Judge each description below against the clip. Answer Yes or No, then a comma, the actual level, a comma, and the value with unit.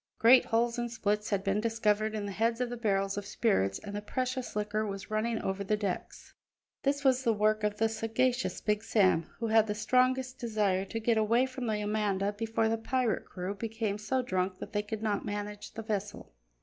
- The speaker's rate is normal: No, fast, 210 wpm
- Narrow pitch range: Yes, narrow, 2.2 semitones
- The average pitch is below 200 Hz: No, high, 215 Hz